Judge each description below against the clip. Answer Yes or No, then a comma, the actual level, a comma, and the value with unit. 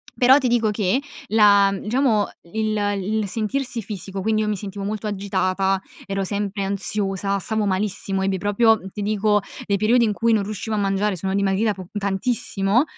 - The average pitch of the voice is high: Yes, high, 205 Hz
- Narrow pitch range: Yes, narrow, 1.9 semitones